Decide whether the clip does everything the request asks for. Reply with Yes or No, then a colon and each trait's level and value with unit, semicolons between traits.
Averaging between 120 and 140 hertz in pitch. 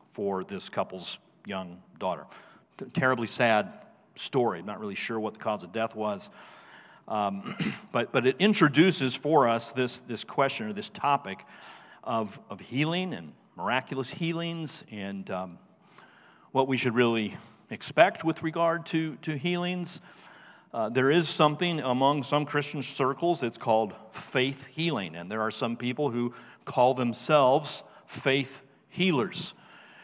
Yes: low, 135 Hz